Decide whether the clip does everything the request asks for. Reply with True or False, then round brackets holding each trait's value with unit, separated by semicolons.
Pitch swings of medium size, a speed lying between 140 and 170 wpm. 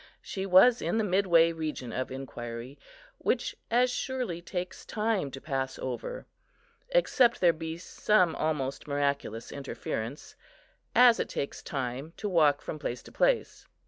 False (7.1 semitones; 145 wpm)